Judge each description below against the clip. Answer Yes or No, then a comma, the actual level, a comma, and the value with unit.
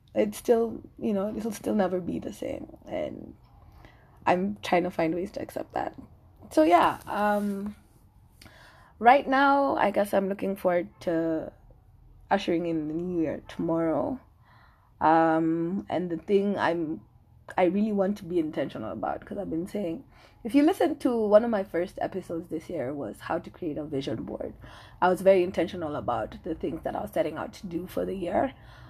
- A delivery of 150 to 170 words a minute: No, average, 180 wpm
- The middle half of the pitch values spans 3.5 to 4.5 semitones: Yes, average, 4.1 semitones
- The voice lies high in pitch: No, medium, 180 Hz